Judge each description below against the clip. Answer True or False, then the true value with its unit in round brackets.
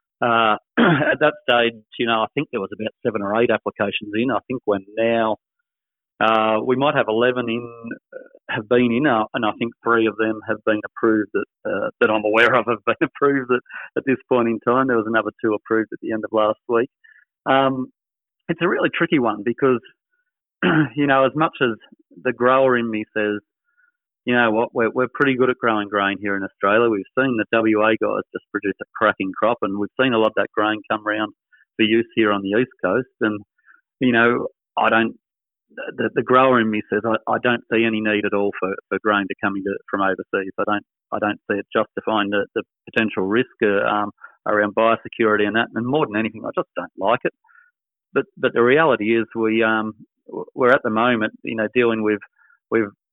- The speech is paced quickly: True (215 wpm)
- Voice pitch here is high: False (115 Hz)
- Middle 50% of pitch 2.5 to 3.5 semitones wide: True (2.8 semitones)